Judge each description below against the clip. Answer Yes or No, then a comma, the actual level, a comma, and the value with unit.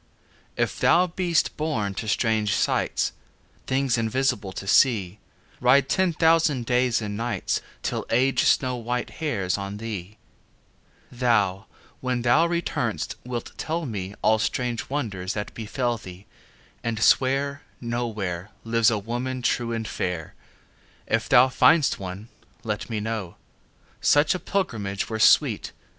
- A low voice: Yes, low, 115 Hz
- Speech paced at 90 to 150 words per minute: Yes, slow, 135 wpm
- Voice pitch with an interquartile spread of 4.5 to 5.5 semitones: No, average, 4.1 semitones